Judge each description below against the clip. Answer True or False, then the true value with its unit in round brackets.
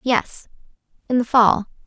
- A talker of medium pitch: False (235 Hz)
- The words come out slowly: True (95 wpm)